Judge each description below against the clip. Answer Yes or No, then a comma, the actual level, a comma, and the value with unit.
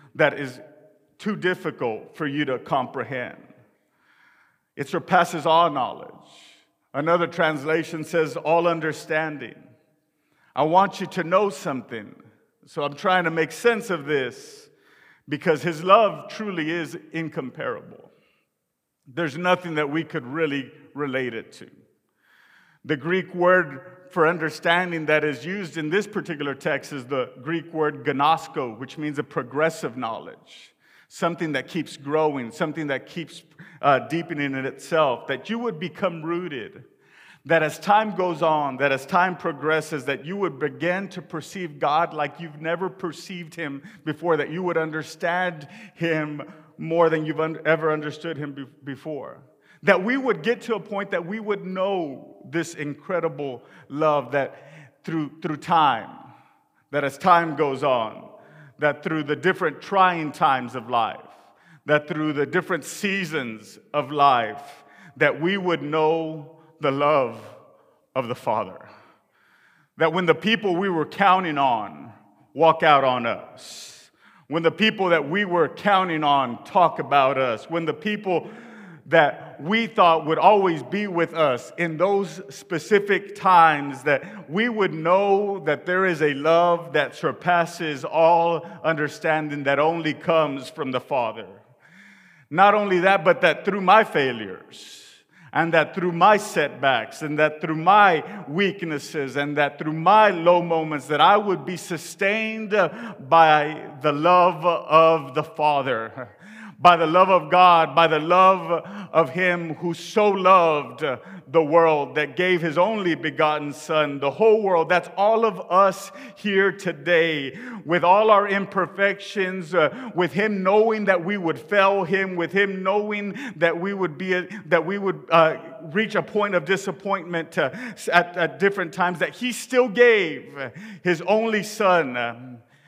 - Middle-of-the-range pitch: Yes, medium, 170 Hz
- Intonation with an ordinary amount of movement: Yes, average, 3.7 semitones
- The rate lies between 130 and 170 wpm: Yes, average, 150 wpm